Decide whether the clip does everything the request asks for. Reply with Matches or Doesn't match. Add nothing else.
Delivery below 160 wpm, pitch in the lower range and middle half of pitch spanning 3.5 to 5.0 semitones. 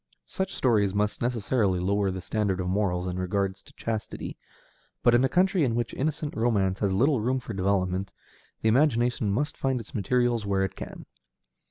Doesn't match